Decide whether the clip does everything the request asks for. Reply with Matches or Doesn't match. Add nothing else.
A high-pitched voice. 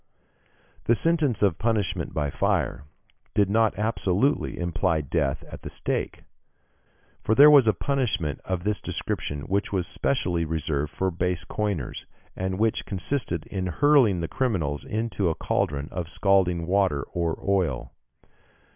Doesn't match